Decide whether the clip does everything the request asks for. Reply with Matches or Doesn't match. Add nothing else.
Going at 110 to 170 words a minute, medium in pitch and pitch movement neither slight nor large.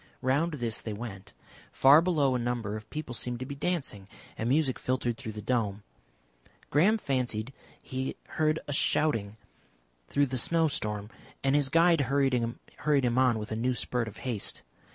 Doesn't match